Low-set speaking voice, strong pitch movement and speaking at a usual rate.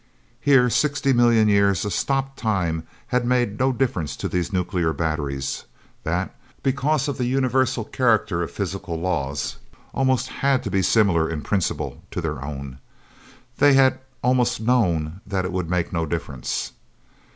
Yes: low, 100 Hz; wide, 7.3 semitones; average, 150 wpm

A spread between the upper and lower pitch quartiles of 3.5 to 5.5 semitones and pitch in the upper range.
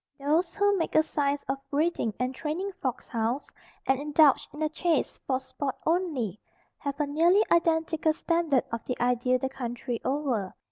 Yes: average, 4.1 semitones; very high, 285 Hz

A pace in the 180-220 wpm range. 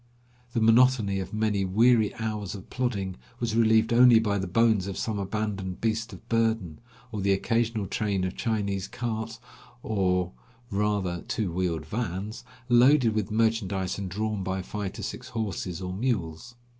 No: average, 160 wpm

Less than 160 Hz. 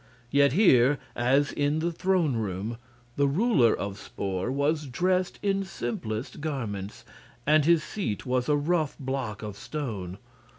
Yes: medium, 140 Hz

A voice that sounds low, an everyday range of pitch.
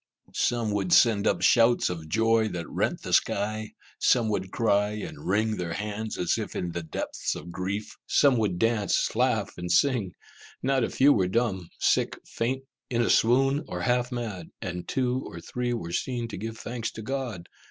Yes: low, 110 Hz; average, 4.5 semitones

